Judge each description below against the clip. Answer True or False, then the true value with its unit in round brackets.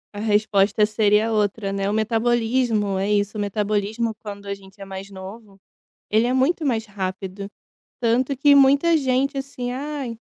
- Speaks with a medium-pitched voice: False (215 Hz)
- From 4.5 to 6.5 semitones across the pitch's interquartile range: False (3.7 semitones)